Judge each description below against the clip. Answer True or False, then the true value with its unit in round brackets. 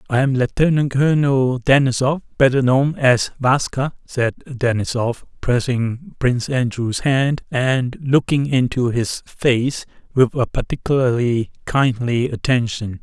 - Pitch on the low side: True (130 Hz)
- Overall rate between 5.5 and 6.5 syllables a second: False (3.9 syllables/s)